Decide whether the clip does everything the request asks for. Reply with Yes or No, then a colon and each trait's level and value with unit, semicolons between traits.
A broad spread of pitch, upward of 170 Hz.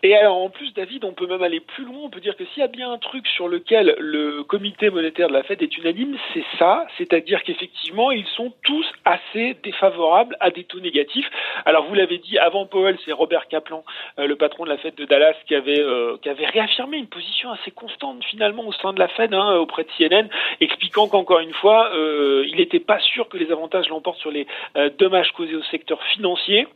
Yes: wide, 6.3 semitones; high, 190 Hz